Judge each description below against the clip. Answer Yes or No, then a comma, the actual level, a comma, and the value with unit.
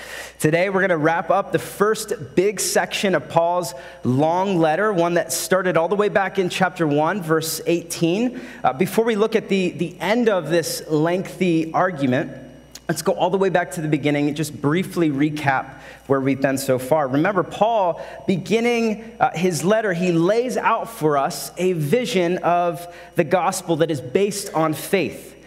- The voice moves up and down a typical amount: Yes, average, 3.4 semitones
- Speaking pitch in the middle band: Yes, medium, 175 Hz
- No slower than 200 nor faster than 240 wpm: No, average, 180 wpm